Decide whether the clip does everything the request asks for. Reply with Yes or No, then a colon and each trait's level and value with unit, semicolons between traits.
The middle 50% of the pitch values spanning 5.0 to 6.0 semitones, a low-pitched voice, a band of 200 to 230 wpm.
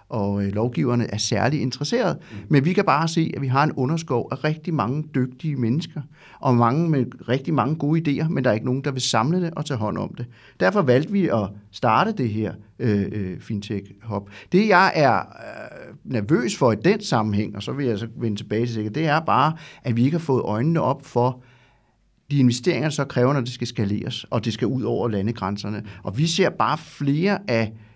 Yes: average, 5.3 semitones; low, 125 Hz; average, 215 wpm